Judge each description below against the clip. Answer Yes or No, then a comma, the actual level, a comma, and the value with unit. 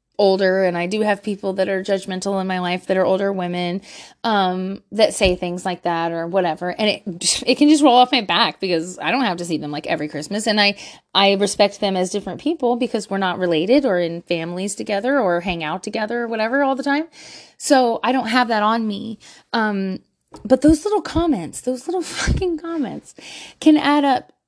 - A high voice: Yes, high, 205 Hz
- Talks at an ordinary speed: No, fast, 215 wpm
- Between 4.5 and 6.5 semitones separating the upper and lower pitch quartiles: Yes, average, 5.3 semitones